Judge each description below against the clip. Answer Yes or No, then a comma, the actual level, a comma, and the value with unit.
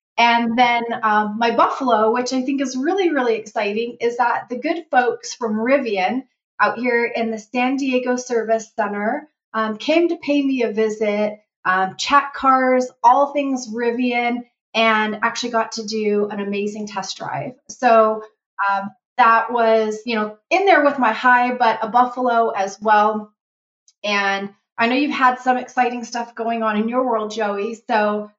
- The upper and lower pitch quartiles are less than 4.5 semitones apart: Yes, average, 2.7 semitones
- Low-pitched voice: No, high, 230 Hz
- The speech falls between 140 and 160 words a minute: No, average, 170 wpm